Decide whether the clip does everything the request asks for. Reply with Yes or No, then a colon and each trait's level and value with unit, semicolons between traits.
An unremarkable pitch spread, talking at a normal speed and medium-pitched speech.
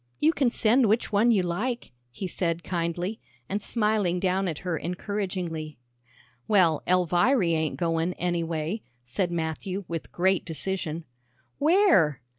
No: average, 3.8 semitones; slow, 130 wpm; medium, 180 Hz